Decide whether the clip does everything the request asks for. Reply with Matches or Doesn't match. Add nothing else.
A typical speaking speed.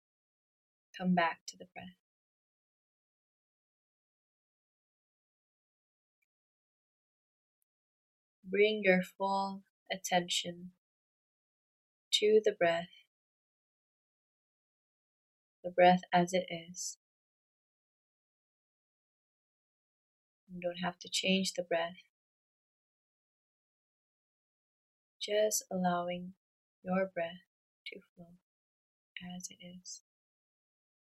Doesn't match